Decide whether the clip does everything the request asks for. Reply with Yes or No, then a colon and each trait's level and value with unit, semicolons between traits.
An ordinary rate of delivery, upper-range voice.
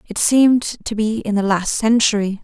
Yes: average, 195 wpm; high, 215 Hz